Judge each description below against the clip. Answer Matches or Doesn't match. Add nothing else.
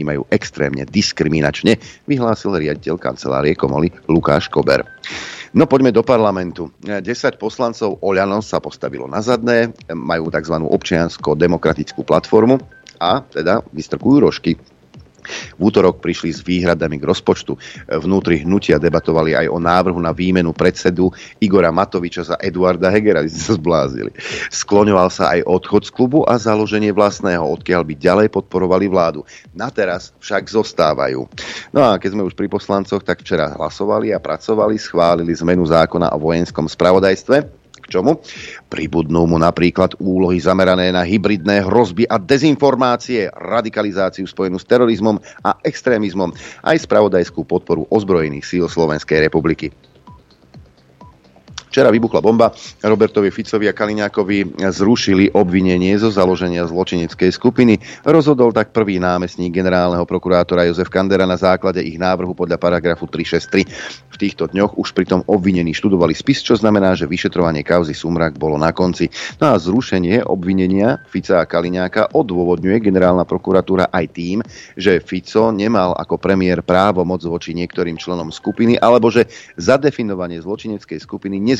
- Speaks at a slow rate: Doesn't match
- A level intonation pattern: Doesn't match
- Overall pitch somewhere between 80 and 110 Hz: Matches